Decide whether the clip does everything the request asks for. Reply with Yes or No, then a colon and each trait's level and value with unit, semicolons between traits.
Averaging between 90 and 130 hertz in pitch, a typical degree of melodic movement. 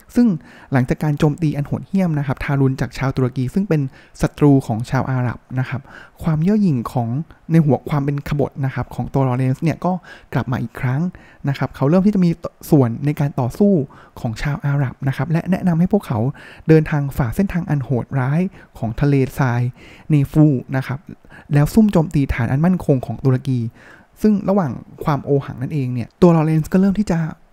No: medium, 140 Hz; average, 4.1 semitones